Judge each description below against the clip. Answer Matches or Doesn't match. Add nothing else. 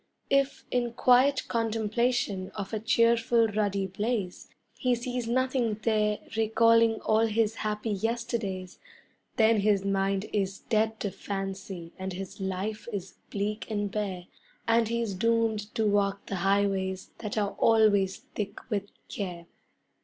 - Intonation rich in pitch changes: Doesn't match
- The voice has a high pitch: Matches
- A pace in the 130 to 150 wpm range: Matches